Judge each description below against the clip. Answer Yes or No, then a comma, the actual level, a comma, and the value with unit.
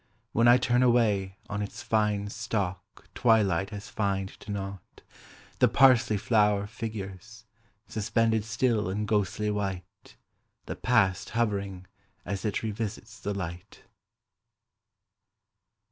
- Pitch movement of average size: No, narrow, 2.3 semitones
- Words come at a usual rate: No, slow, 115 wpm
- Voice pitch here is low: Yes, low, 105 Hz